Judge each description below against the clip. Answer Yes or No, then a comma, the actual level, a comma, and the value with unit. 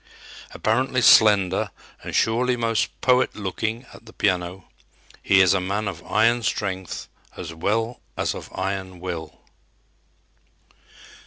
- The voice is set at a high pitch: No, low, 100 Hz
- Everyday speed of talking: No, slow, 125 wpm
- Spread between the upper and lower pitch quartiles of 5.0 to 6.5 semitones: No, average, 3.5 semitones